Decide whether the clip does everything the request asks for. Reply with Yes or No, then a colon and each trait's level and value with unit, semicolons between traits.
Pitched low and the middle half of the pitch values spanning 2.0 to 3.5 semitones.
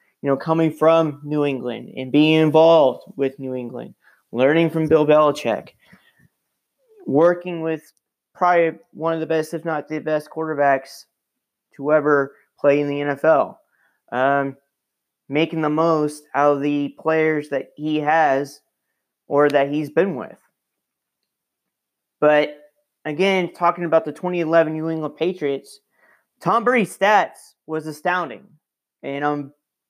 No: medium, 155 Hz; narrow, 2.4 semitones